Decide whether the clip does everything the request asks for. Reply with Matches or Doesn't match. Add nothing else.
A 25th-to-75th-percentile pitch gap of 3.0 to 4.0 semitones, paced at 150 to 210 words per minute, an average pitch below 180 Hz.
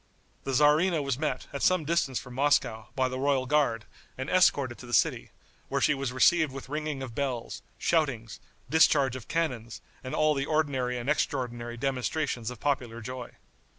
Matches